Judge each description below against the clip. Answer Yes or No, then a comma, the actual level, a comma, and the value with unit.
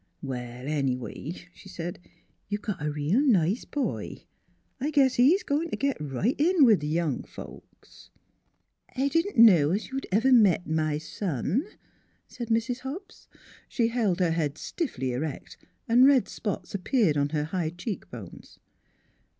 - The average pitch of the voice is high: Yes, high, 195 Hz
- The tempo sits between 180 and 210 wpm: No, average, 160 wpm